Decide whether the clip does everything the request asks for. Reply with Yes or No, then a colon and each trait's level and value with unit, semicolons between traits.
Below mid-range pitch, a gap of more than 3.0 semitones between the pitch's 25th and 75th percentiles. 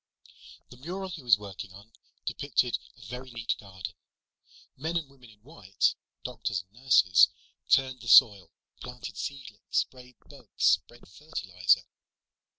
Yes: low, 120 Hz; average, 5.0 semitones